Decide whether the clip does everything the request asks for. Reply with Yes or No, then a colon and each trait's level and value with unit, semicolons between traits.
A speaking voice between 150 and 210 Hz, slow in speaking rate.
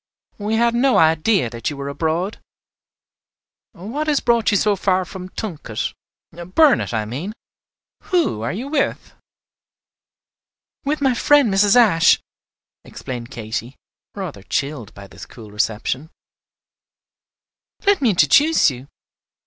Yes: medium, 185 Hz; slow, 125 wpm